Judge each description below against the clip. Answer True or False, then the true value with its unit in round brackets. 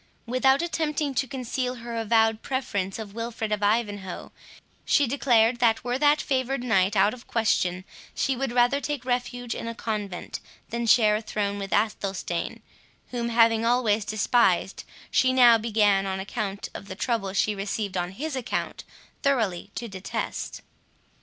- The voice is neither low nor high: False (230 Hz)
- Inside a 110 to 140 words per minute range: False (155 wpm)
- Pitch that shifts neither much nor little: True (3.6 semitones)